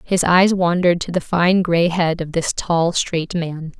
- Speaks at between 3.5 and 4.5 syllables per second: Yes, 4.1 syllables/s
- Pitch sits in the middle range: Yes, medium, 170 Hz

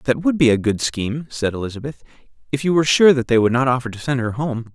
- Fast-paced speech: Yes, fast, 265 wpm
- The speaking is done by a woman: No, male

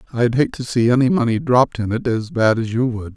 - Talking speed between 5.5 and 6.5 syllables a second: Yes, 5.8 syllables/s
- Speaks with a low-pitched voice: Yes, low, 120 Hz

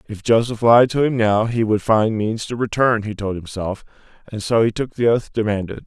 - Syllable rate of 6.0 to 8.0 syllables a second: No, 5.1 syllables/s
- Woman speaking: No, male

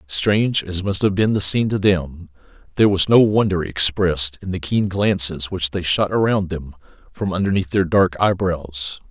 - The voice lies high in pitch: No, very low, 90 Hz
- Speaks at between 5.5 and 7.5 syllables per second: No, 4.9 syllables/s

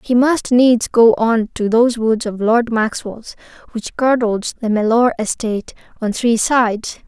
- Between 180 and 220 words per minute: No, average, 160 wpm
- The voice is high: Yes, high, 230 Hz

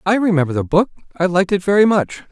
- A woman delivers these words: No, male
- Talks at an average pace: No, fast, 235 wpm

